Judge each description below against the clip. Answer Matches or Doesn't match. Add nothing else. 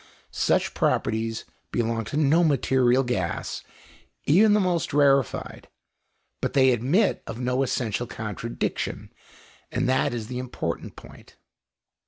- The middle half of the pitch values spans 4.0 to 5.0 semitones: Doesn't match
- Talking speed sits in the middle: Doesn't match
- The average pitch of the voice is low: Matches